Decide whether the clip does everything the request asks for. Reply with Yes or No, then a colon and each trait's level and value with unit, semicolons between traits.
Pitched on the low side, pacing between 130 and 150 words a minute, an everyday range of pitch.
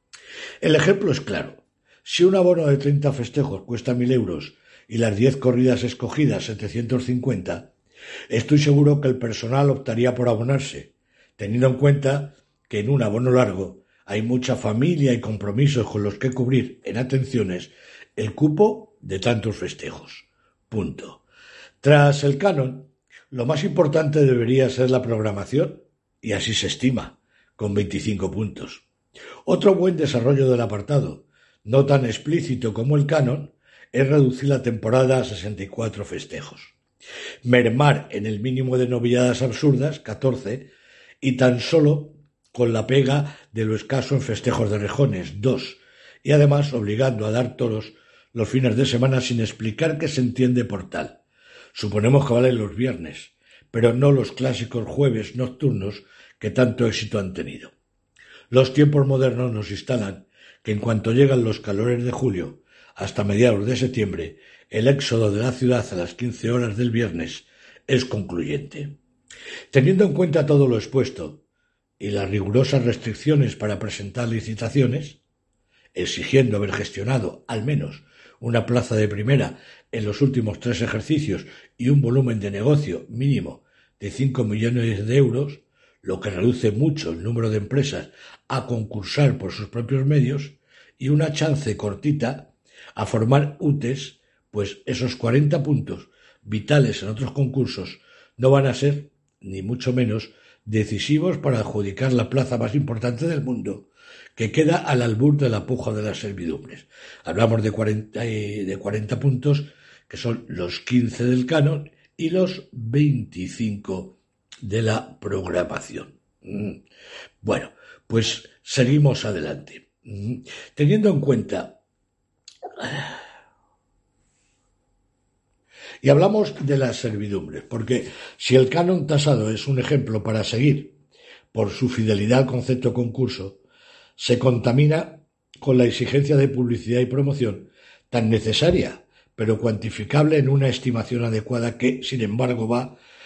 Yes: low, 125 Hz; average, 140 wpm; average, 4.1 semitones